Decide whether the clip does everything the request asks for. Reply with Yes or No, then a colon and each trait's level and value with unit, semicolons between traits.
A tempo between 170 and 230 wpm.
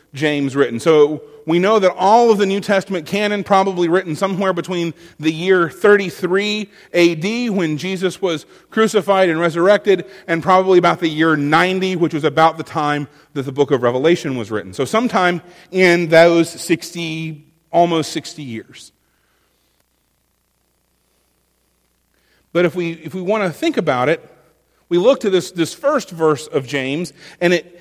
No: average, 160 wpm